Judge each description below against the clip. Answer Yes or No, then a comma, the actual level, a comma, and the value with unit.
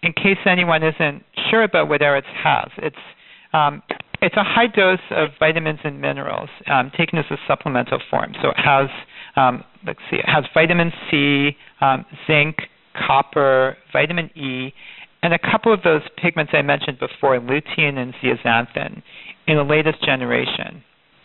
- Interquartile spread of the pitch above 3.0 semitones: Yes, average, 3.5 semitones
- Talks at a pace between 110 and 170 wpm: Yes, average, 160 wpm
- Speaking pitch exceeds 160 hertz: No, medium, 155 Hz